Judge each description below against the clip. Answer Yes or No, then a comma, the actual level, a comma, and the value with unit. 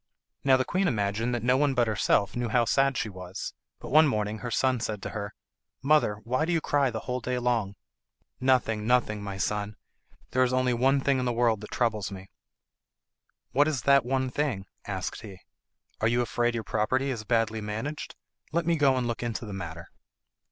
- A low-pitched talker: Yes, low, 120 Hz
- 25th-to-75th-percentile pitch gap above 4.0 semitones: No, average, 3.7 semitones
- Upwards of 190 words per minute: Yes, average, 200 wpm